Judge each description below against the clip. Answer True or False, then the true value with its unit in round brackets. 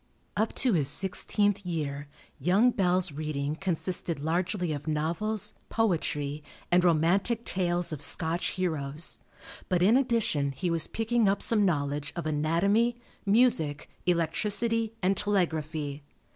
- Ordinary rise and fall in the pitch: True (5.0 semitones)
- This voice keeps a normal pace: False (125 wpm)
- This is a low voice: False (175 Hz)